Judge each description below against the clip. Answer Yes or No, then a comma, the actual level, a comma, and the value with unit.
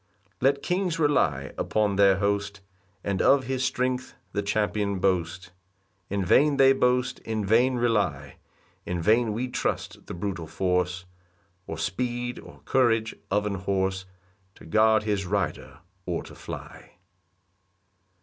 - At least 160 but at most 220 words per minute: No, average, 140 wpm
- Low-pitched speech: Yes, low, 105 Hz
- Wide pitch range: No, average, 4.6 semitones